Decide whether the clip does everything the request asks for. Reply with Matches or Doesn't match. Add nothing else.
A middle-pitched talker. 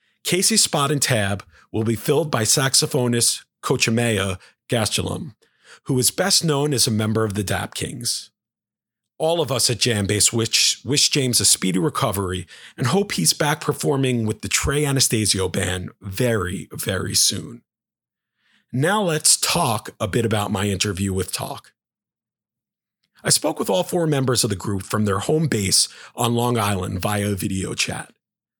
Doesn't match